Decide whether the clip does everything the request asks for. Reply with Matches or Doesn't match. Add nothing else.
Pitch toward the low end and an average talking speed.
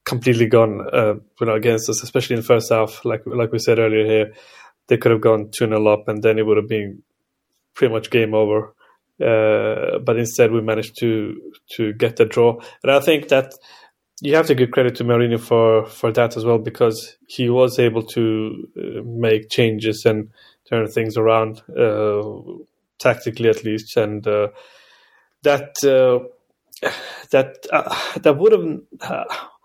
Matches